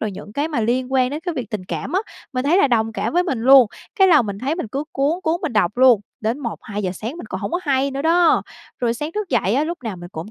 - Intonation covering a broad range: Yes, wide, 6.1 semitones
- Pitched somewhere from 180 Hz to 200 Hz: No, very high, 260 Hz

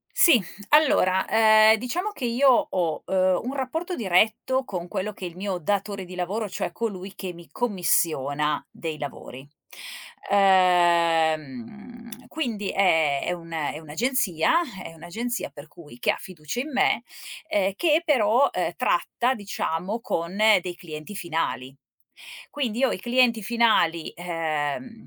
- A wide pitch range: Yes, wide, 6.1 semitones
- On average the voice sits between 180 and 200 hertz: Yes, high, 190 Hz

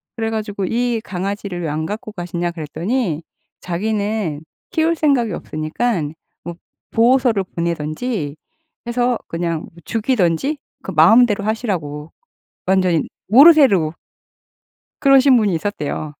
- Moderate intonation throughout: No, wide, 6.1 semitones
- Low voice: No, high, 200 Hz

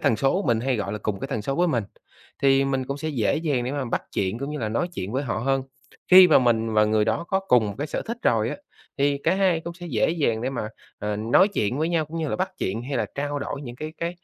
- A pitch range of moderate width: No, wide, 5.8 semitones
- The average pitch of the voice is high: No, low, 135 Hz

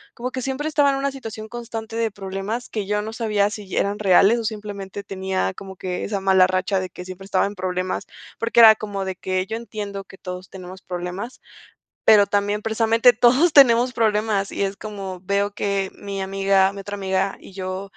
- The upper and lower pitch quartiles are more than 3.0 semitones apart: No, average, 2.7 semitones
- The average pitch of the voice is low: No, high, 200 Hz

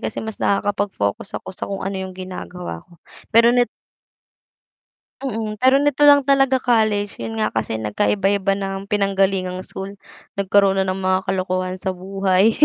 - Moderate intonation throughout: No, narrow, 2.3 semitones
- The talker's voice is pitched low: No, high, 195 Hz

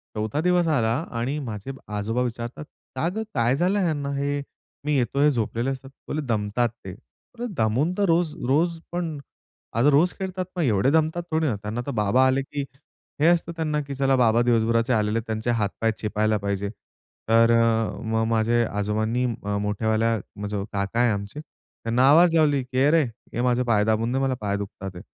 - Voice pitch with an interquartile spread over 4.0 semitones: Yes, average, 5.1 semitones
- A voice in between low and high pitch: No, low, 120 Hz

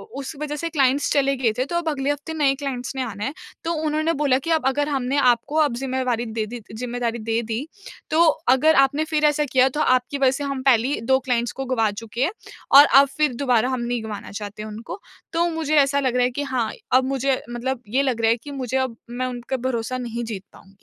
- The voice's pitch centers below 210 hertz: No, very high, 260 Hz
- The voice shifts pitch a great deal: No, average, 3.1 semitones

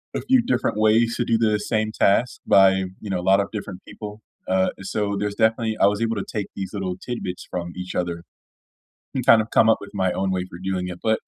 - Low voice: Yes, low, 100 Hz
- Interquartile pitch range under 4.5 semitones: Yes, average, 2.8 semitones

